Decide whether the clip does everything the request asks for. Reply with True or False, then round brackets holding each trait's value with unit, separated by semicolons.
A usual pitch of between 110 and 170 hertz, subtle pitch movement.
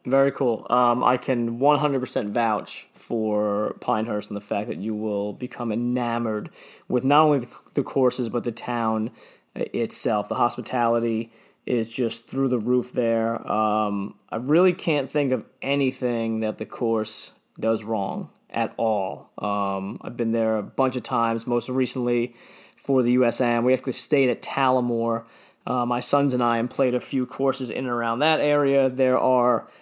True (120 Hz; 2.3 semitones)